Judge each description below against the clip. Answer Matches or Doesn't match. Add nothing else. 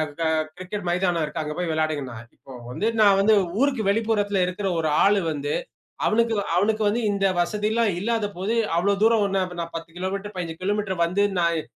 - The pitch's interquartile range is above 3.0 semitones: Matches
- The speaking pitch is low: Doesn't match